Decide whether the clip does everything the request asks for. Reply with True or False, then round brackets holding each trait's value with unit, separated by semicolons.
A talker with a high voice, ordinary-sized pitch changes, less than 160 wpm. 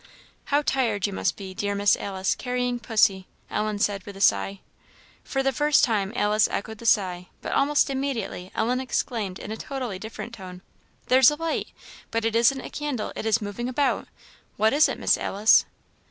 False (220 Hz; 4.4 semitones; 185 wpm)